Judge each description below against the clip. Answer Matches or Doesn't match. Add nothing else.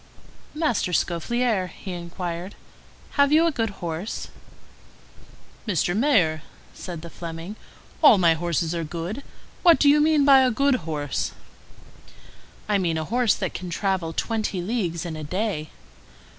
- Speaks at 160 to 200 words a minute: Doesn't match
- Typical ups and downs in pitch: Doesn't match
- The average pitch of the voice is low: Doesn't match